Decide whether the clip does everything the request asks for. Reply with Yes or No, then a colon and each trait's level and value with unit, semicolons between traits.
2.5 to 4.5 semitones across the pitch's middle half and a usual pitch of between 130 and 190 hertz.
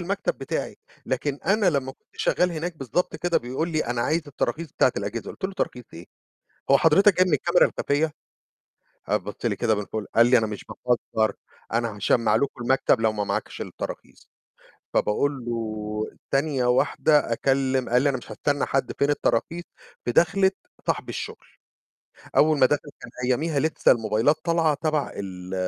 No: average, 5.0 semitones; low, 135 Hz